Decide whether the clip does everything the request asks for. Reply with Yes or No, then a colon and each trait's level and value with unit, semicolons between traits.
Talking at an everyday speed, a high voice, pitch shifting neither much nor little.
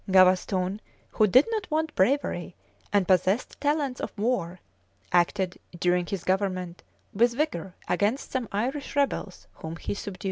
No: average, 145 wpm; high, 200 Hz; wide, 5.8 semitones